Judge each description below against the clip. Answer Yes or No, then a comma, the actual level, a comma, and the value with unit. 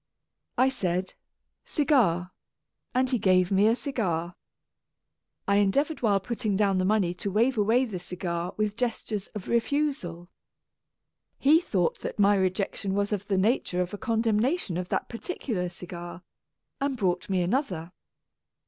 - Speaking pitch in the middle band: No, high, 200 Hz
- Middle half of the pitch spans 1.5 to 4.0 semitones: No, average, 4.8 semitones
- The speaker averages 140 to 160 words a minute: Yes, average, 150 wpm